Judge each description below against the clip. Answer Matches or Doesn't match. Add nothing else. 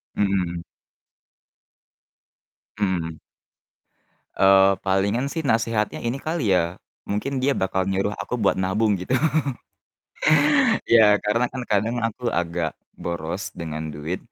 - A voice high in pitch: Doesn't match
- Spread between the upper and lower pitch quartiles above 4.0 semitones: Matches